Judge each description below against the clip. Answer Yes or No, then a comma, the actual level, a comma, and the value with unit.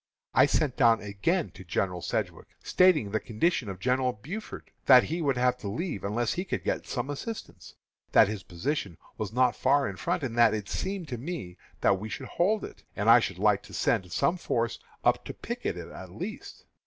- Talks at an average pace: No, fast, 210 wpm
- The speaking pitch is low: Yes, low, 120 Hz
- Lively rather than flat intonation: Yes, wide, 6.4 semitones